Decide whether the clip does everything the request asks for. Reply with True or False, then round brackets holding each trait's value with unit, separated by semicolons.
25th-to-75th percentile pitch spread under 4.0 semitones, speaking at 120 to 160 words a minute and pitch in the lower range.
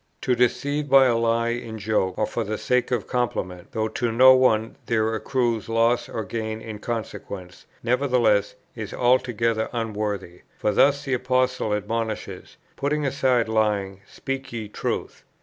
True (2.7 semitones; 150 wpm; 115 Hz)